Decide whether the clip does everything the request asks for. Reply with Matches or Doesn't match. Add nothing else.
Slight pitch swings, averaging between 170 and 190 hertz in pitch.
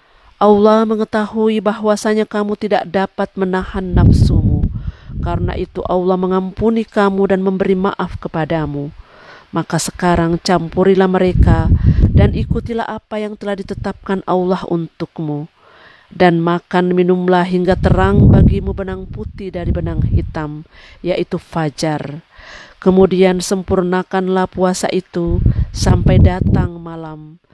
Doesn't match